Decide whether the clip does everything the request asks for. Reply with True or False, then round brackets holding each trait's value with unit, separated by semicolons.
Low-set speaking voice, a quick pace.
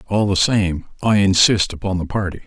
False (95 Hz; 195 wpm)